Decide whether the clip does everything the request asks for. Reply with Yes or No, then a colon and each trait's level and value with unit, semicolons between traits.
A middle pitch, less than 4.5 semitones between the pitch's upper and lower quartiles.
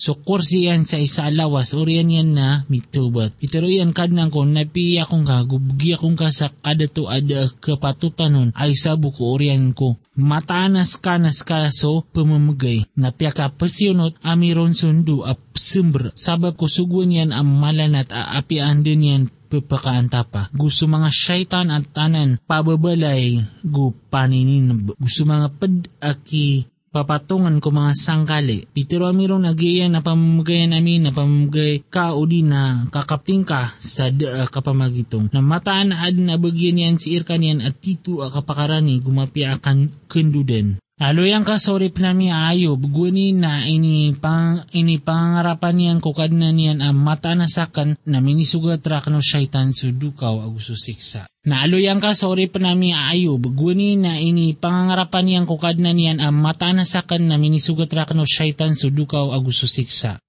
Yes: medium, 155 Hz; average, 3.5 semitones